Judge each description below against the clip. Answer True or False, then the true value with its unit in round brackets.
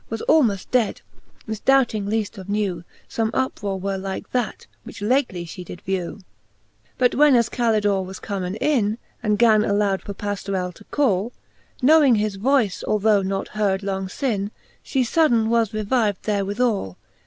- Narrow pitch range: False (3.2 semitones)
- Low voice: False (210 Hz)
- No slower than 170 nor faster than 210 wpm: False (155 wpm)